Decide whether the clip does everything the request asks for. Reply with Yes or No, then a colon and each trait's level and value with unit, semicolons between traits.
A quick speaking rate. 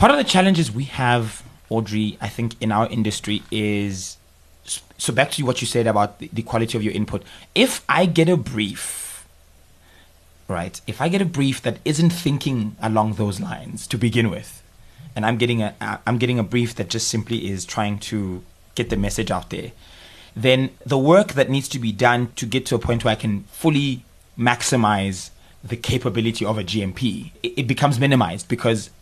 No: average, 190 wpm